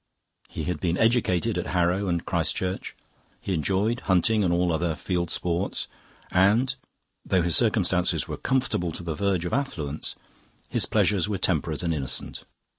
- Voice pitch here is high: No, very low, 90 Hz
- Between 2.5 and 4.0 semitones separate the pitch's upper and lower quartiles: Yes, average, 2.8 semitones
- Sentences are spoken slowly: No, average, 160 wpm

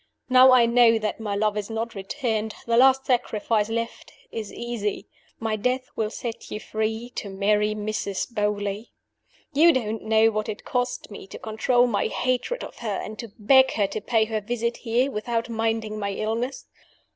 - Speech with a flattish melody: Yes, narrow, 2.3 semitones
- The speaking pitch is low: No, high, 225 Hz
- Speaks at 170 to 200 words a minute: Yes, average, 180 wpm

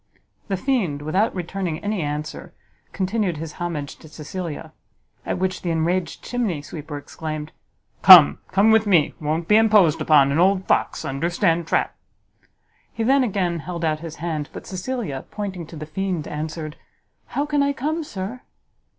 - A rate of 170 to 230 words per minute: No, average, 160 wpm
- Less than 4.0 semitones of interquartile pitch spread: No, average, 4.8 semitones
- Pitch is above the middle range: No, medium, 175 Hz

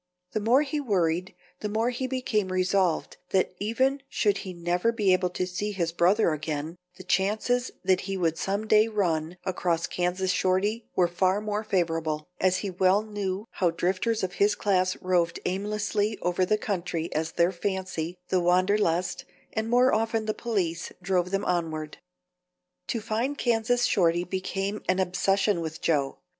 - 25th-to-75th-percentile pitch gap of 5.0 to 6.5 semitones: No, average, 3.3 semitones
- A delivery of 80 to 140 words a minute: No, average, 165 wpm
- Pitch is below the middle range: No, high, 190 Hz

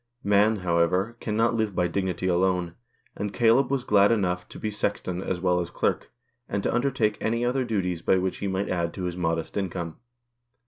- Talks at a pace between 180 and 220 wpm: Yes, average, 190 wpm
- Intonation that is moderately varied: Yes, average, 3.5 semitones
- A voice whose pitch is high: No, very low, 95 Hz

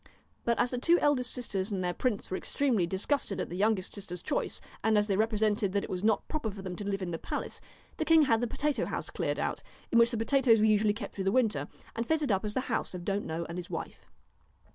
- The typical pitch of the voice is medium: No, high, 215 Hz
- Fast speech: Yes, fast, 260 wpm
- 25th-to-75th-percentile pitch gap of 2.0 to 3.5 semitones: No, average, 4.0 semitones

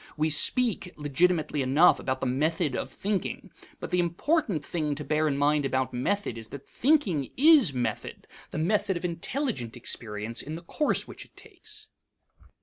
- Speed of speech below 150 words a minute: No, average, 165 wpm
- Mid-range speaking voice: Yes, medium, 155 Hz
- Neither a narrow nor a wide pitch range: No, wide, 7.0 semitones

